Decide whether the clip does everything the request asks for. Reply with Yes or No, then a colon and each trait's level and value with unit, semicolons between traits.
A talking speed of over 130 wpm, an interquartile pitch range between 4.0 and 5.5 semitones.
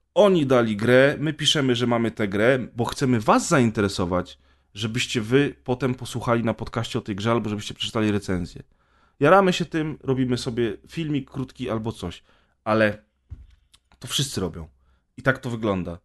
Yes: fast, 160 wpm; average, 4.5 semitones